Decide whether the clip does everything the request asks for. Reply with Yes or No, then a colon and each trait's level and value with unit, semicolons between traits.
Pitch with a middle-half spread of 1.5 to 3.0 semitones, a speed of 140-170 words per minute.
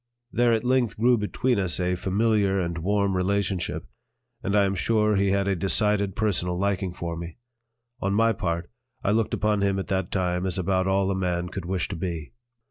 No: narrow, 2.5 semitones; average, 200 wpm